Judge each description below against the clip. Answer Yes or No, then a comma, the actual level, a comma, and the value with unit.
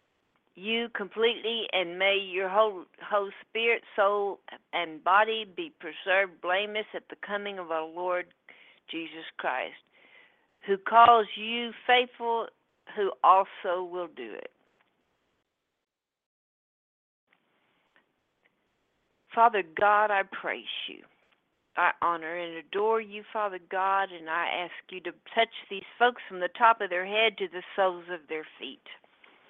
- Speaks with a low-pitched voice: No, high, 200 Hz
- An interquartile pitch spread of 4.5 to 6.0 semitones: No, average, 3.9 semitones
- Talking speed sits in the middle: No, slow, 130 wpm